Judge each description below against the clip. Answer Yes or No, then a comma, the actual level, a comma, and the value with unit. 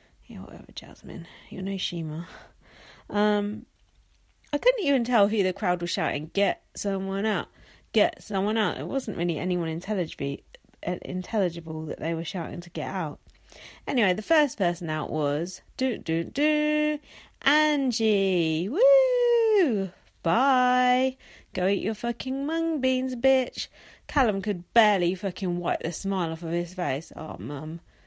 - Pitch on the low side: No, high, 200 Hz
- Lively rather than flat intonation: Yes, wide, 6.8 semitones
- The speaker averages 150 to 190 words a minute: No, average, 140 wpm